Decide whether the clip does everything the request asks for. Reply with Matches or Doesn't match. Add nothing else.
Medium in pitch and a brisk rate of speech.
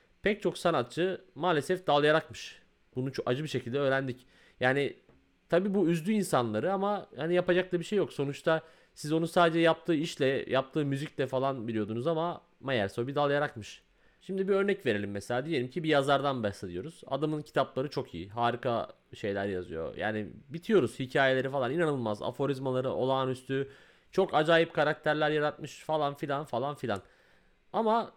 Matches